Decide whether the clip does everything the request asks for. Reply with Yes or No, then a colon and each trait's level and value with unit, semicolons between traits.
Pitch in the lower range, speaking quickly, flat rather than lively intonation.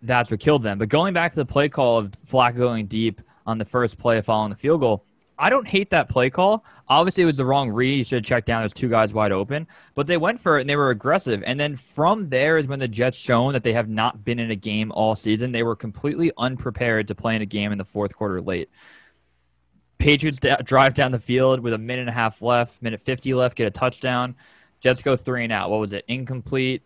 No: low, 125 Hz; fast, 255 wpm; average, 3.7 semitones